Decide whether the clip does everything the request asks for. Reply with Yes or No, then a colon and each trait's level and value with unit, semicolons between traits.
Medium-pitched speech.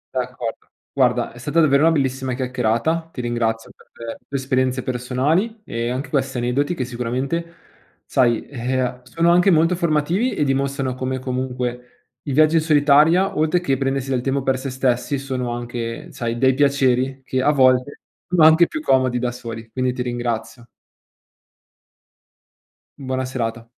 No: low, 130 Hz